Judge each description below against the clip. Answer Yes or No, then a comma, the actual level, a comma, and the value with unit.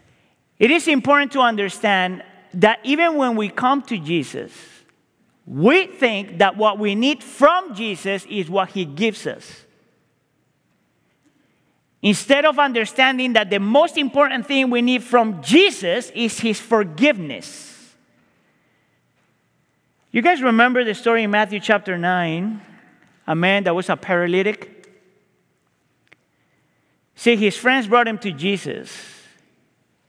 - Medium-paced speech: No, slow, 125 wpm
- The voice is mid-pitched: No, high, 220 Hz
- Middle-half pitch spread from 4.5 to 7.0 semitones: Yes, average, 4.8 semitones